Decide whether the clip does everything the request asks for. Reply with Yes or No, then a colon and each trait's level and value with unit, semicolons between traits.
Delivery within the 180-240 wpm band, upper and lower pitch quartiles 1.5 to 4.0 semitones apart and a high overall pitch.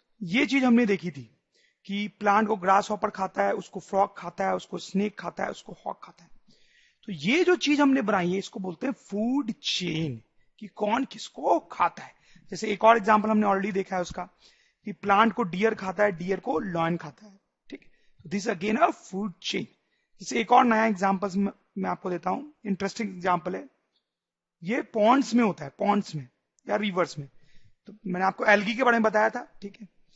Yes: fast, 205 wpm; average, 3.3 semitones; high, 205 Hz